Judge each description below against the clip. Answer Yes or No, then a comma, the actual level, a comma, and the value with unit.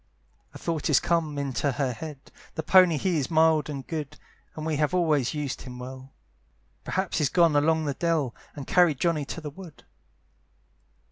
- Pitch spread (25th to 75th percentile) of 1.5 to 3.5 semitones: Yes, average, 2.9 semitones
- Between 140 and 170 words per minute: No, average, 180 wpm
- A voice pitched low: No, medium, 150 Hz